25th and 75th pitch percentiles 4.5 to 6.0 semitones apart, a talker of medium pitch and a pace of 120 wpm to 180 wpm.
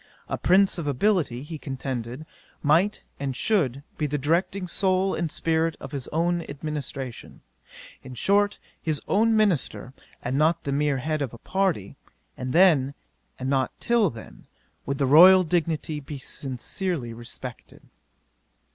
Yes: average, 5.2 semitones; medium, 150 Hz; average, 145 wpm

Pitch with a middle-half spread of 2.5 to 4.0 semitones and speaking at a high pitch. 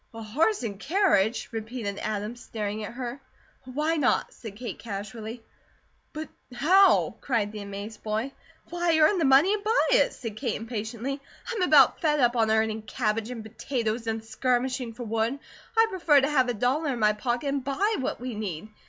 No: average, 4.5 semitones; high, 240 Hz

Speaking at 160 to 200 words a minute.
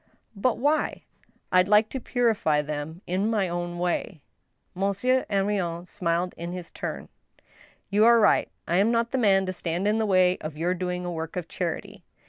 Yes: average, 180 wpm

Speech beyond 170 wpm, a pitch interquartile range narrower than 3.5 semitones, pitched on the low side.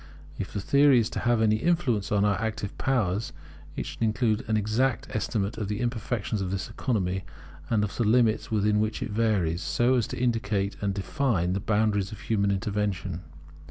Yes: average, 190 wpm; average, 2.7 semitones; low, 105 Hz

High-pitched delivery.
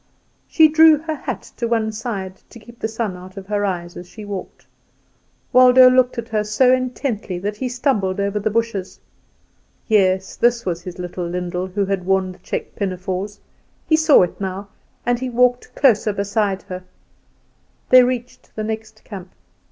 Yes: high, 210 Hz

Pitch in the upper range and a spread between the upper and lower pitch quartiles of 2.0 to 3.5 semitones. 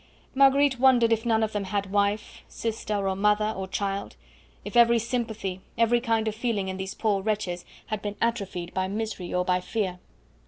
Yes: high, 210 Hz; average, 3.0 semitones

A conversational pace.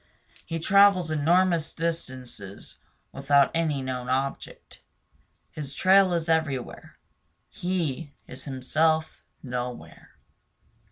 No: slow, 90 wpm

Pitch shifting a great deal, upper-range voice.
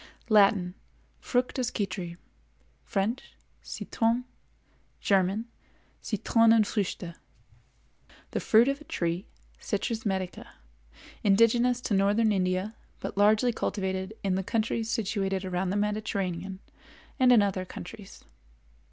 No: average, 3.2 semitones; high, 205 Hz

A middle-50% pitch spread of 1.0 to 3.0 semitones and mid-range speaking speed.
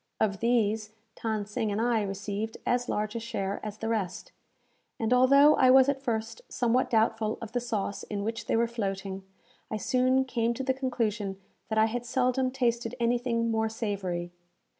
Yes: narrow, 2.6 semitones; average, 180 wpm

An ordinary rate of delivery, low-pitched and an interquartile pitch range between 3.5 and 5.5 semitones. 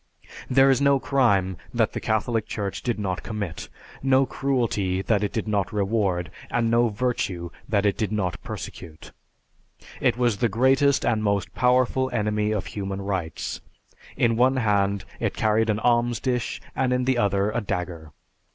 Yes: average, 165 wpm; low, 110 Hz; average, 3.9 semitones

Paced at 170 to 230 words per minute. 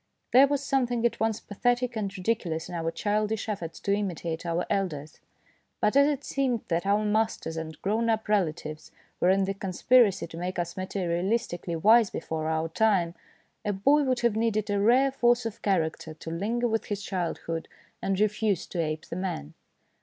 Yes: average, 185 wpm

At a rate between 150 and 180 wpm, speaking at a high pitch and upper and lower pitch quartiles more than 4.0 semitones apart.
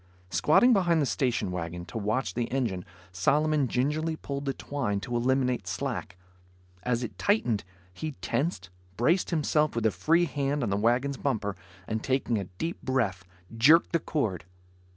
No: average, 160 wpm; low, 130 Hz; average, 5.3 semitones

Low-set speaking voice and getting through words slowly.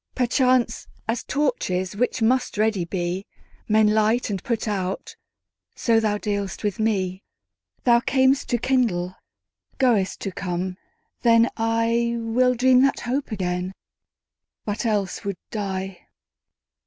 No: high, 220 Hz; slow, 115 wpm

